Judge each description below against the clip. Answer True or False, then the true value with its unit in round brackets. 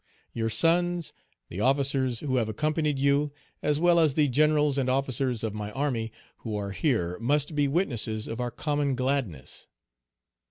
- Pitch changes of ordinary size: True (4.6 semitones)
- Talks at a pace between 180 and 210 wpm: False (160 wpm)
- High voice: False (135 Hz)